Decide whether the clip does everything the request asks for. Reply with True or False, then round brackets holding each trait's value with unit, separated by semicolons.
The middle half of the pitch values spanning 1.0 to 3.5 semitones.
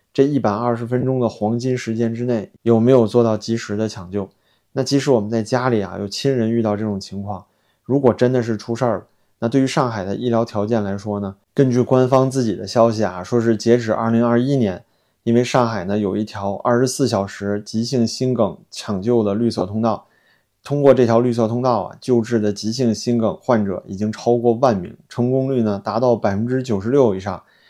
True (3.0 semitones)